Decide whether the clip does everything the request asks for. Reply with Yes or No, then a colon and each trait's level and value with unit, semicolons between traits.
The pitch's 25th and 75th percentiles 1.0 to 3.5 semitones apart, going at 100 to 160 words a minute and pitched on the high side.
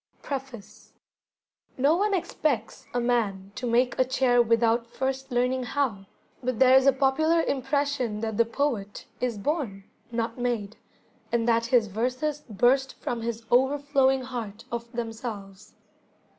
Yes: average, 2.7 semitones; average, 140 wpm; high, 245 Hz